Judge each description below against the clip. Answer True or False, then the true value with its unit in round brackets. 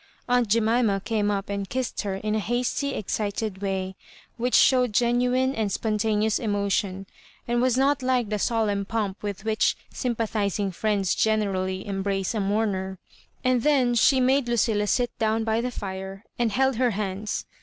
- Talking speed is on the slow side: False (165 wpm)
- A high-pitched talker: True (215 Hz)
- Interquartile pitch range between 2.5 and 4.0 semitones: True (3.3 semitones)